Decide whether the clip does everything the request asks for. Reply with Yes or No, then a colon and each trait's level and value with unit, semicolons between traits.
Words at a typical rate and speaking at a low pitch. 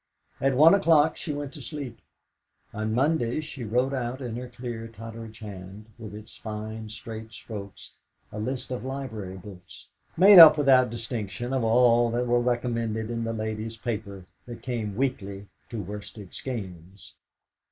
Yes: average, 155 wpm; low, 115 Hz